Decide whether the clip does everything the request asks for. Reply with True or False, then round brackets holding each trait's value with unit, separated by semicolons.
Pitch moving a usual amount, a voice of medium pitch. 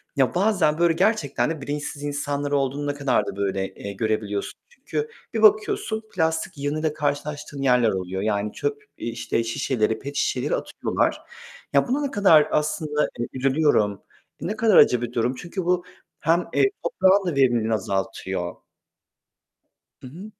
False (6.8 semitones; 145 Hz)